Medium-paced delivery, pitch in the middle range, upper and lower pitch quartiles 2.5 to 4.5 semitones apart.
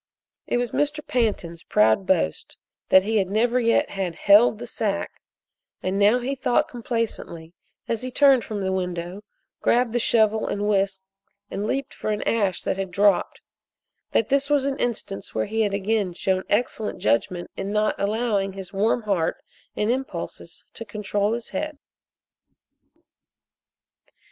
No: average, 155 wpm; high, 210 Hz; average, 3.5 semitones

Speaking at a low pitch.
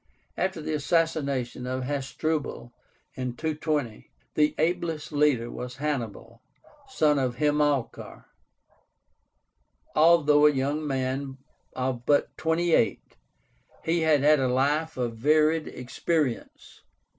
No: medium, 145 Hz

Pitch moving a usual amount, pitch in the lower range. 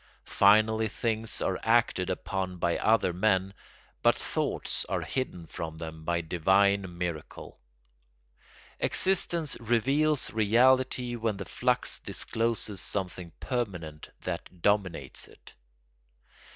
Yes: average, 4.6 semitones; low, 100 Hz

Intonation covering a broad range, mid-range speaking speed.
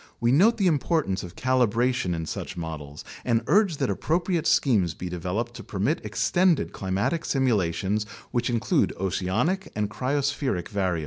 Yes: wide, 7.4 semitones; average, 155 wpm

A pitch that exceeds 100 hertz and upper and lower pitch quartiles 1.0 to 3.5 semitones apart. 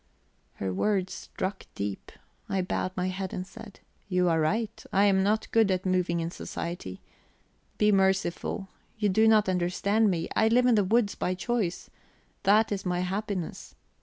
Yes: high, 190 Hz; narrow, 2.6 semitones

